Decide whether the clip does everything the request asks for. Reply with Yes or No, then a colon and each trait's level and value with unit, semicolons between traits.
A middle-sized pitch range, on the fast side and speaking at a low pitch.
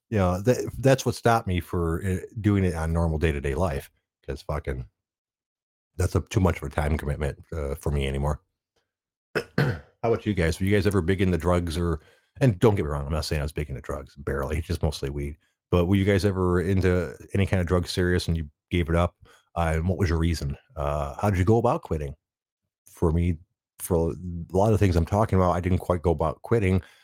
Yes: average, 3.5 semitones; fast, 235 wpm; very low, 90 Hz